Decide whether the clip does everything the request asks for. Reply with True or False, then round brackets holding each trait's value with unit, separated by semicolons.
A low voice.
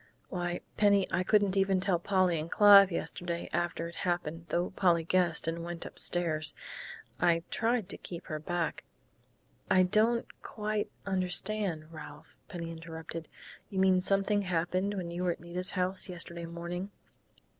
False (175 Hz)